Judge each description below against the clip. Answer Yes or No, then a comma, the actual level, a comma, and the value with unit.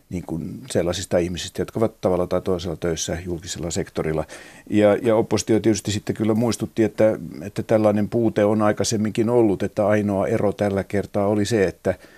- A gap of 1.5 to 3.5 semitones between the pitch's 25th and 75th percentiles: Yes, average, 2.9 semitones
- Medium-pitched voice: No, low, 105 Hz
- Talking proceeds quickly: Yes, fast, 170 wpm